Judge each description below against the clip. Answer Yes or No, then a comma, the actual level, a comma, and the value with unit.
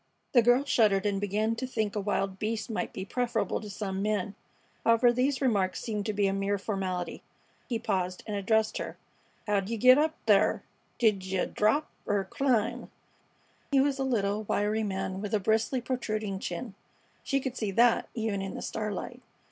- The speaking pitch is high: Yes, high, 215 Hz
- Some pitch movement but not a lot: Yes, average, 3.2 semitones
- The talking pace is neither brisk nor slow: Yes, average, 180 wpm